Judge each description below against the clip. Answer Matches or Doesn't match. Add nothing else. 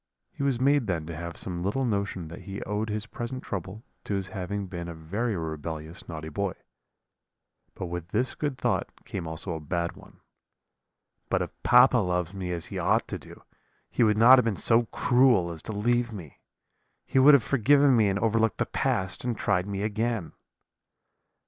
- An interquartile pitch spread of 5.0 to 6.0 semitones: Matches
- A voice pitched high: Doesn't match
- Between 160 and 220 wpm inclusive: Matches